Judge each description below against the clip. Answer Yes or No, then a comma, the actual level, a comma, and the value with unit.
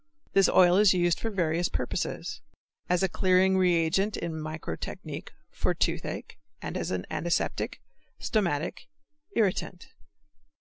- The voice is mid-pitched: Yes, medium, 180 Hz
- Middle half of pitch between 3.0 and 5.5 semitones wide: No, narrow, 2.5 semitones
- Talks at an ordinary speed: No, slow, 110 wpm